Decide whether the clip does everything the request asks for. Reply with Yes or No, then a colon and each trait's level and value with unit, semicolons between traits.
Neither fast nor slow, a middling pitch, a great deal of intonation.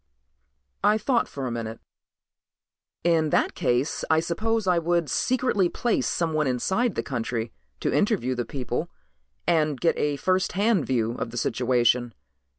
Yes: average, 150 wpm; medium, 155 Hz; wide, 7.1 semitones